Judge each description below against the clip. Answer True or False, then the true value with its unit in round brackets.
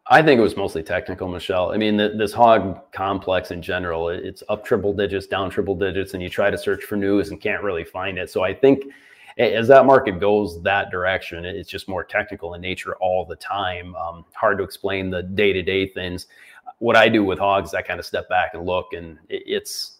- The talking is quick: True (225 wpm)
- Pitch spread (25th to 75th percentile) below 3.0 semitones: True (2.6 semitones)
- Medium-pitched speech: False (95 Hz)